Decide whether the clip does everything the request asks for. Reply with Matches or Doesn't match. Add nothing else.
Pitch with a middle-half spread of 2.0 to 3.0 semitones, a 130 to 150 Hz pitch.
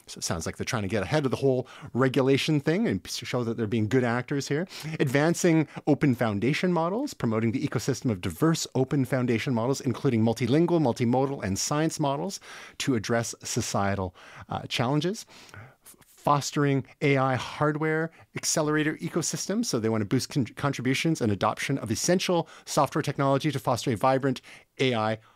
Doesn't match